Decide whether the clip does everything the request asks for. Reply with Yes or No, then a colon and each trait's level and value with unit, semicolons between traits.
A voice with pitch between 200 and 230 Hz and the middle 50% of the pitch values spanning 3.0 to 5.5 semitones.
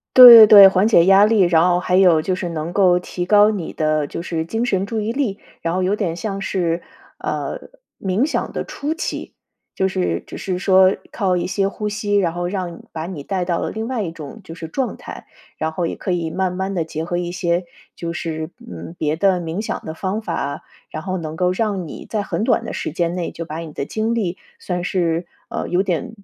No: medium, 185 Hz; average, 3.3 semitones